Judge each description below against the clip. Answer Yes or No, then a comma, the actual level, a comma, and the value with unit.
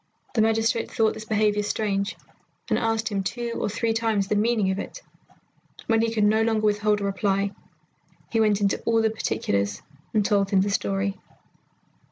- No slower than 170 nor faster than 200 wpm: Yes, average, 180 wpm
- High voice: Yes, high, 210 Hz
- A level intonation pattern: Yes, narrow, 2.0 semitones